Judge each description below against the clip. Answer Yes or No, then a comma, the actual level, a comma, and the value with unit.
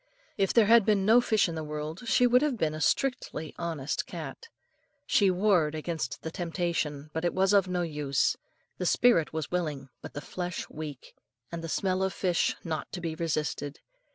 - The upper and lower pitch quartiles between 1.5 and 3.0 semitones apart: No, average, 3.9 semitones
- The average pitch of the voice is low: No, medium, 170 Hz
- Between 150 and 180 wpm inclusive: No, average, 190 wpm